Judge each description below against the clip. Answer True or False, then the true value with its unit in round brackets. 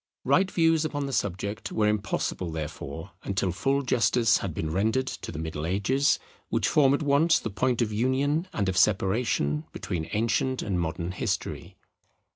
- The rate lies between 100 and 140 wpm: False (165 wpm)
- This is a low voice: True (105 Hz)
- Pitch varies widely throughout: True (6.9 semitones)